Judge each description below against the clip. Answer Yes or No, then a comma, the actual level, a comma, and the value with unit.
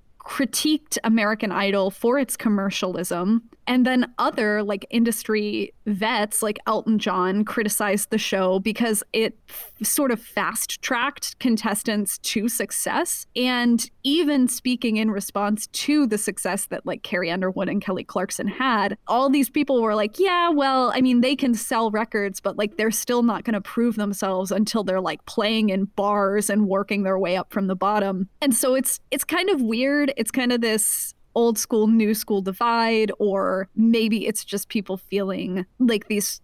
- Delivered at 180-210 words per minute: No, average, 170 wpm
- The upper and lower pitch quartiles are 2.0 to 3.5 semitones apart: Yes, average, 3.2 semitones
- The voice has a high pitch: Yes, high, 220 Hz